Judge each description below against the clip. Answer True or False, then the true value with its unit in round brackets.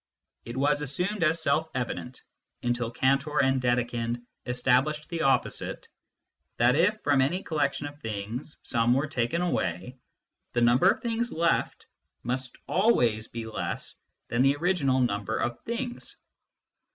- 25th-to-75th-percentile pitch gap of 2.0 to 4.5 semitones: False (4.9 semitones)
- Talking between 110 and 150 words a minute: True (140 wpm)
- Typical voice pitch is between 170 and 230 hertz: False (135 Hz)